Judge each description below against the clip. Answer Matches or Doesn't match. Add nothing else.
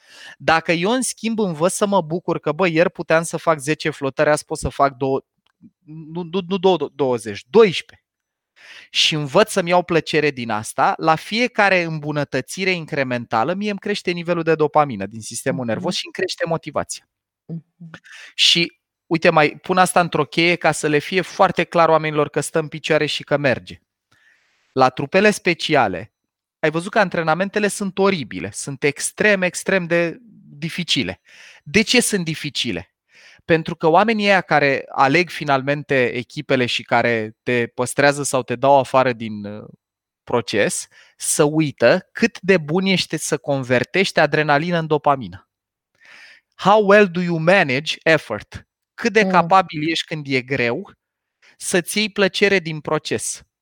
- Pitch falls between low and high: Matches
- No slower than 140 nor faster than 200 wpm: Matches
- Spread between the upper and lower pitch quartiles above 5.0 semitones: Doesn't match